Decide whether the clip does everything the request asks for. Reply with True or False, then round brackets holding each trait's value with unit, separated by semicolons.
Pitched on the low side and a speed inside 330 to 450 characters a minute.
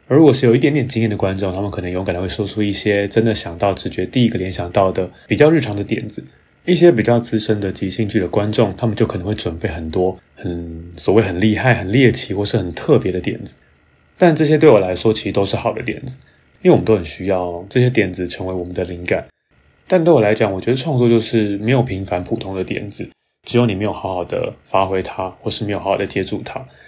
True (105 Hz; 360 characters per minute)